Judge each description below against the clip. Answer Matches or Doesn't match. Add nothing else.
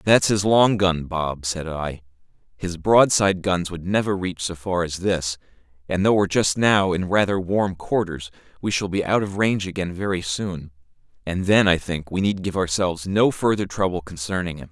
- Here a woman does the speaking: Doesn't match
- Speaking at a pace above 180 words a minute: Matches